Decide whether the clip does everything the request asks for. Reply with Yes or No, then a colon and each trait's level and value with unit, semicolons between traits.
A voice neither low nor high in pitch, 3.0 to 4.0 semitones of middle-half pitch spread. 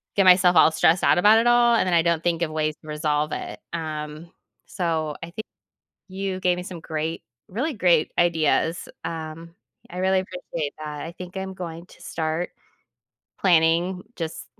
No: medium, 170 Hz; narrow, 2.6 semitones